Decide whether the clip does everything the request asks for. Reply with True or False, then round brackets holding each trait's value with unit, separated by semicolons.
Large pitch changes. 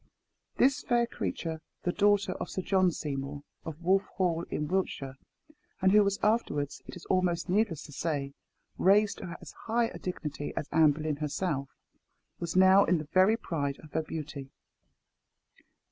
False (4.5 semitones)